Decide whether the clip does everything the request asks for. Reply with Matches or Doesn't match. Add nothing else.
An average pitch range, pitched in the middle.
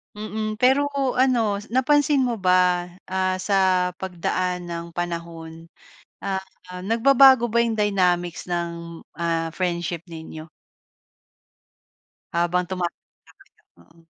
Matches